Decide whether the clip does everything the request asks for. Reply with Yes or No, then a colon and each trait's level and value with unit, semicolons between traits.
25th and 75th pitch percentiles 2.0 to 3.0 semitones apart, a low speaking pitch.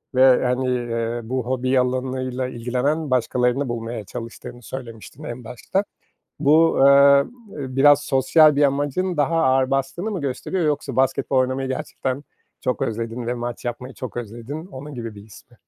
Yes: narrow, 2.6 semitones; low, 130 Hz